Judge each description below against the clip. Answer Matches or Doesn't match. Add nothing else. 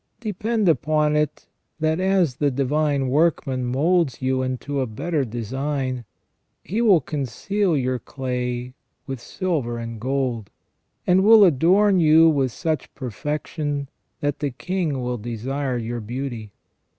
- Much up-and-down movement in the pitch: Doesn't match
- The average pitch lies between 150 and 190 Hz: Doesn't match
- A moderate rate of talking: Doesn't match